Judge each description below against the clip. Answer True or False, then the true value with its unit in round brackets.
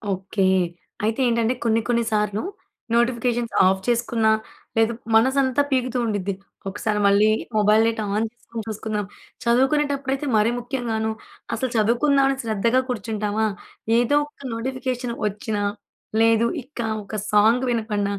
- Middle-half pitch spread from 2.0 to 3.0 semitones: True (2.7 semitones)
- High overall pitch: True (230 Hz)